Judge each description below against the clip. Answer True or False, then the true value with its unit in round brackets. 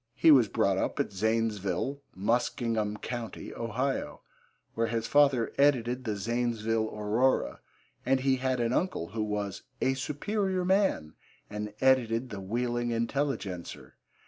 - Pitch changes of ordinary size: True (3.7 semitones)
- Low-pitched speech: True (115 Hz)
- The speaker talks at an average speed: False (130 wpm)